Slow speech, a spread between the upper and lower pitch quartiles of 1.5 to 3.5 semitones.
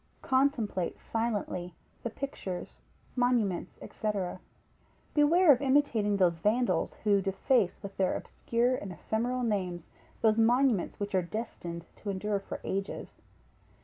No: slow, 120 wpm; average, 4.5 semitones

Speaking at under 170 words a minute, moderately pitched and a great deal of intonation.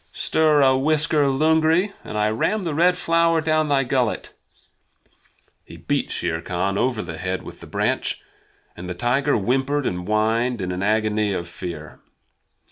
No: average, 160 wpm; low, 125 Hz; wide, 7.9 semitones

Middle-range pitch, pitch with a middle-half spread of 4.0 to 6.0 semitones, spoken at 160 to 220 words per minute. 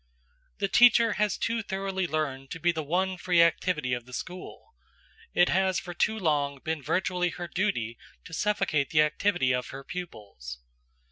Yes: medium, 175 Hz; average, 5.1 semitones; average, 165 wpm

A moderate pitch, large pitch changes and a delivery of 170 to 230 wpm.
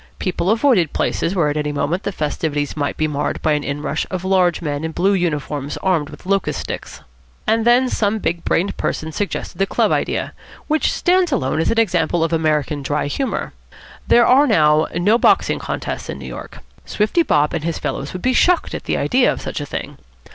Yes: medium, 170 Hz; wide, 6.0 semitones; fast, 205 wpm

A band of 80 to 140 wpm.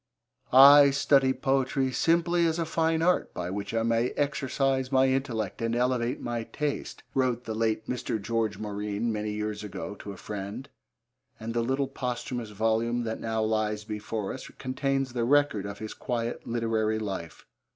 No: average, 165 wpm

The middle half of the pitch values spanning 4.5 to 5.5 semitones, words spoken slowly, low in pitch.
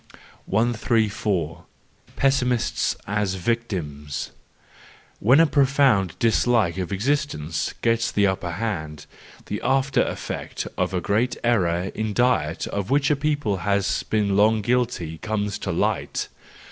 Yes: average, 4.8 semitones; slow, 120 wpm; low, 105 Hz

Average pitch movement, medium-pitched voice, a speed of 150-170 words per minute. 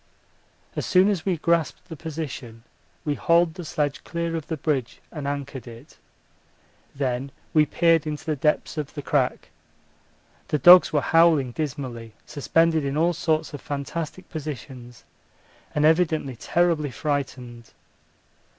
No: average, 3.2 semitones; medium, 150 Hz; average, 140 wpm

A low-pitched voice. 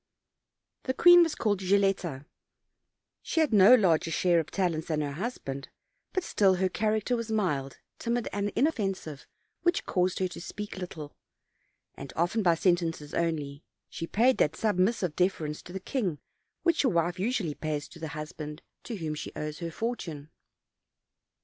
No: medium, 180 Hz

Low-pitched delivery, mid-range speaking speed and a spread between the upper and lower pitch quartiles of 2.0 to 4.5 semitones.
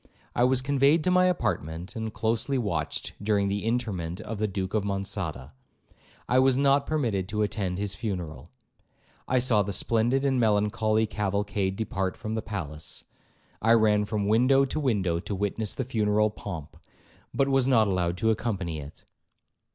Yes: low, 105 Hz; average, 165 wpm; average, 4.0 semitones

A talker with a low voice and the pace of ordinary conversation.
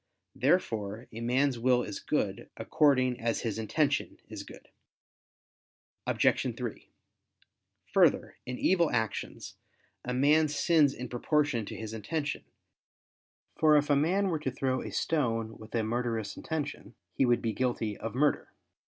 Yes: low, 125 Hz; average, 145 wpm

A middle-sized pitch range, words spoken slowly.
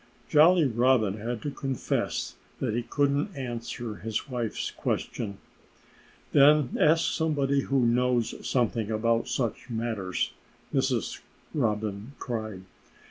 Yes: average, 3.9 semitones; slow, 110 wpm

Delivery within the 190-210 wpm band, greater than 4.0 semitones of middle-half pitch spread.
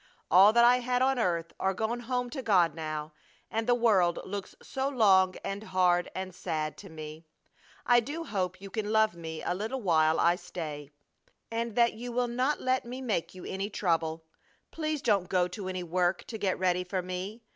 Yes: average, 200 wpm; average, 5.2 semitones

